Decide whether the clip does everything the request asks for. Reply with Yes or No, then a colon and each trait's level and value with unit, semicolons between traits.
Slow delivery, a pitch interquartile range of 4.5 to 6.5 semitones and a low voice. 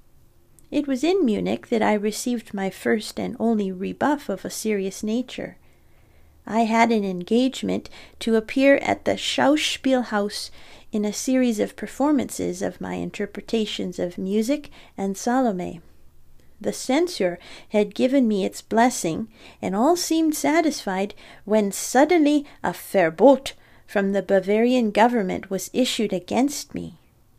No: slow, 130 wpm; average, 5.0 semitones; high, 225 Hz